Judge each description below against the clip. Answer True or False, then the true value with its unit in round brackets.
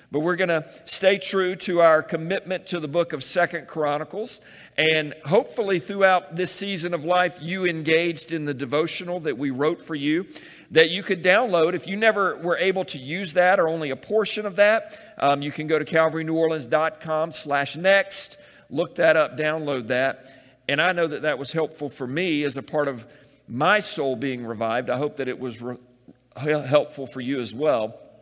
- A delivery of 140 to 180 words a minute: False (195 wpm)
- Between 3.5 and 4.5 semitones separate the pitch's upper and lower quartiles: True (3.9 semitones)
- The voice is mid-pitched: True (160 Hz)